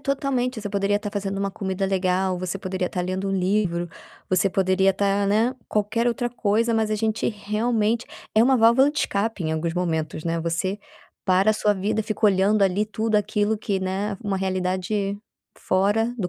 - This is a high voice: Yes, high, 200 Hz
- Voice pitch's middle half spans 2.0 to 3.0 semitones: Yes, narrow, 2.6 semitones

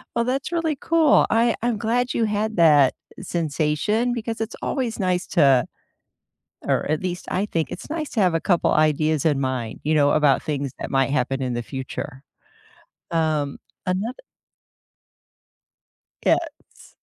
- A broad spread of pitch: Yes, wide, 7.8 semitones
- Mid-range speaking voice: Yes, medium, 170 Hz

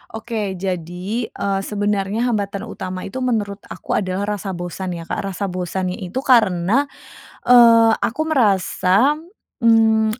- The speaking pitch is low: No, high, 205 Hz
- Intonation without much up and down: No, average, 3.5 semitones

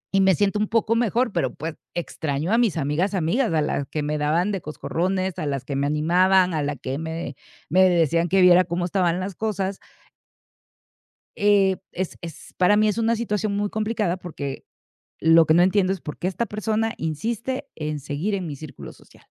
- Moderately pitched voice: Yes, medium, 180 Hz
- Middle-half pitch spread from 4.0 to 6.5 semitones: Yes, average, 4.7 semitones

